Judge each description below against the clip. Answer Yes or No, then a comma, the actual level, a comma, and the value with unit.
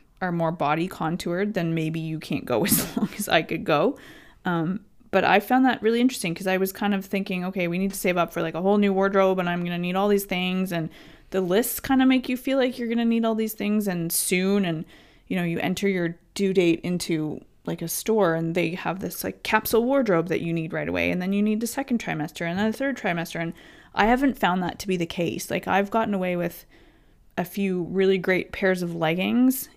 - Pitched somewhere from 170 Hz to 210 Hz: Yes, high, 190 Hz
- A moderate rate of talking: No, fast, 245 wpm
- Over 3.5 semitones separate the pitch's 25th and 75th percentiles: Yes, average, 3.9 semitones